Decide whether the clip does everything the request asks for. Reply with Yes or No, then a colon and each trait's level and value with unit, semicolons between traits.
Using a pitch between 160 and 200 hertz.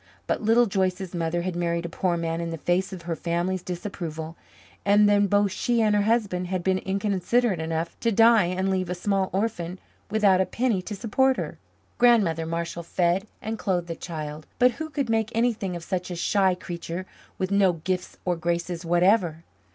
Yes: medium, 185 Hz